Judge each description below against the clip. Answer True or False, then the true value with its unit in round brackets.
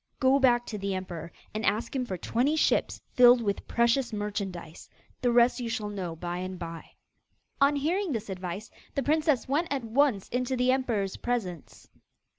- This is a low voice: False (235 Hz)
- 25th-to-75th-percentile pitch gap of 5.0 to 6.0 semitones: True (5.3 semitones)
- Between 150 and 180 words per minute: True (175 wpm)